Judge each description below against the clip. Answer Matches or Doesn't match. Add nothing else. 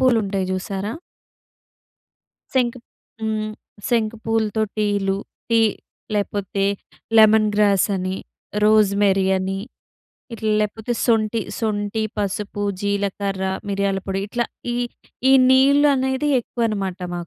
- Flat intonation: Matches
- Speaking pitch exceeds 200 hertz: Matches